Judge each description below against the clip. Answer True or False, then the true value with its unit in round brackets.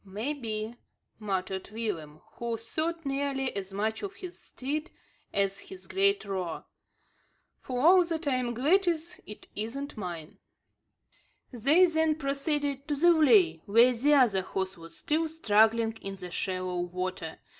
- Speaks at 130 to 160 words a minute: True (140 wpm)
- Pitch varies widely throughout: True (7.7 semitones)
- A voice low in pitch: False (240 Hz)